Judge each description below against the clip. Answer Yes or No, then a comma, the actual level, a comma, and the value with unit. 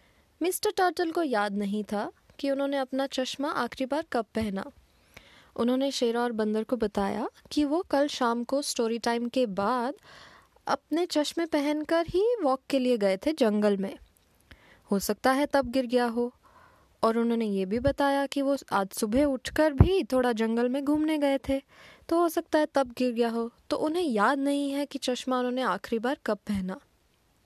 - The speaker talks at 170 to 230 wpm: Yes, average, 185 wpm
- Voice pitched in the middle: No, very high, 265 Hz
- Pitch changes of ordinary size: Yes, average, 4.1 semitones